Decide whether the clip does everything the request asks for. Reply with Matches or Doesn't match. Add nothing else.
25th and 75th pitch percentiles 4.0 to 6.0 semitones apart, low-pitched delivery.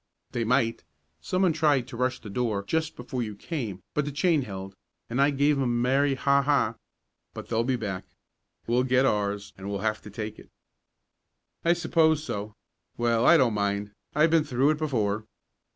Matches